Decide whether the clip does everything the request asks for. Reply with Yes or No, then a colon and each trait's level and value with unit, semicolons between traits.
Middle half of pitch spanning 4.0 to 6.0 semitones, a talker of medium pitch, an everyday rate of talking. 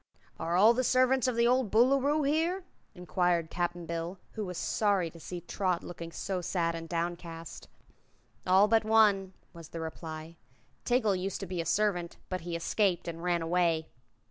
Yes: average, 4.5 semitones; medium, 180 Hz; average, 170 wpm